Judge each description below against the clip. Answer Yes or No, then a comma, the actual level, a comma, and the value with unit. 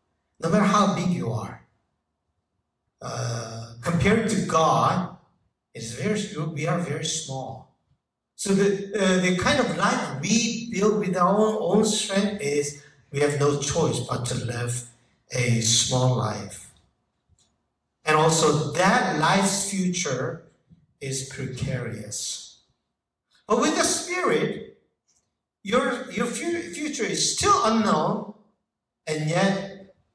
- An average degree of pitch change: No, wide, 8.4 semitones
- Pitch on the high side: No, medium, 165 Hz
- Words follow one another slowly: Yes, slow, 120 wpm